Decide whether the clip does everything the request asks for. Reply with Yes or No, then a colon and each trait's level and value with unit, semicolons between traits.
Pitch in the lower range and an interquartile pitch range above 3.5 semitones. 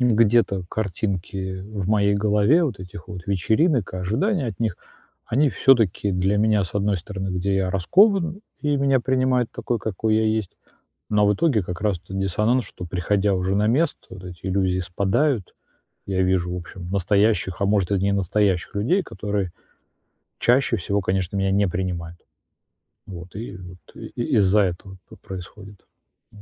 No: low, 100 Hz; average, 3.0 semitones